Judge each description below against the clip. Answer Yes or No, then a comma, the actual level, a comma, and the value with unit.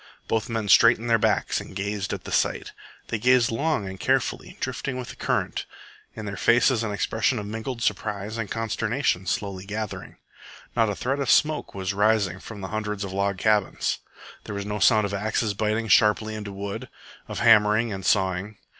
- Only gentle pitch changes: Yes, narrow, 2.2 semitones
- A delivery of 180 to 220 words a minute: Yes, average, 185 wpm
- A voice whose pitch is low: Yes, low, 105 Hz